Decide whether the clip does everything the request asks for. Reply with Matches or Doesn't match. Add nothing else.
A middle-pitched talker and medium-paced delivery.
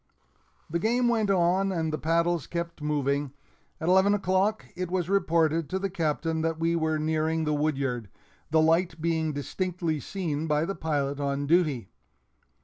Matches